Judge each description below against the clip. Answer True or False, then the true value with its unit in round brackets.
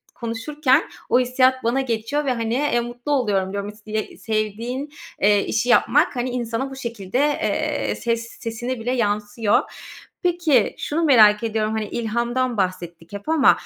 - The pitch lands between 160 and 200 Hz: False (235 Hz)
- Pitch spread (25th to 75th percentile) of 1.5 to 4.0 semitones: True (3.3 semitones)